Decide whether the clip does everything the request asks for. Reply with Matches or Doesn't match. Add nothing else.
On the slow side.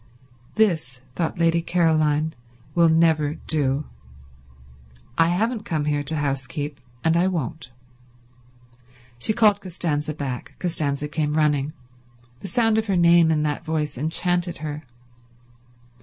Matches